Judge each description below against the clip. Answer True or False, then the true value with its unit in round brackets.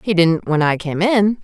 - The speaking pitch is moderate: True (180 Hz)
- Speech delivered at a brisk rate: True (250 wpm)